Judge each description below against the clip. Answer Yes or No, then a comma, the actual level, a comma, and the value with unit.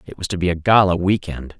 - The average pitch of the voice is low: Yes, very low, 90 Hz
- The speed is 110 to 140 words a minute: No, fast, 265 wpm